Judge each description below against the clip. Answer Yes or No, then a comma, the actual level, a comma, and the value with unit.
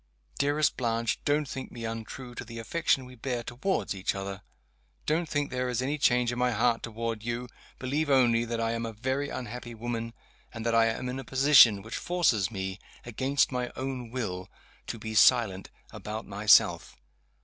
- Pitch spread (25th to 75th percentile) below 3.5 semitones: Yes, narrow, 2.6 semitones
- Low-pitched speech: Yes, low, 120 Hz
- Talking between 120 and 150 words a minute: No, average, 180 wpm